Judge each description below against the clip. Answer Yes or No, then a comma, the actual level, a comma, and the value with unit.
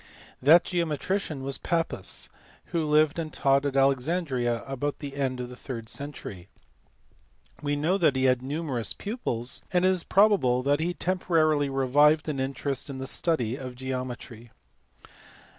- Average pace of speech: Yes, average, 150 wpm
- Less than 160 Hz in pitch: Yes, medium, 140 Hz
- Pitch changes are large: No, average, 3.8 semitones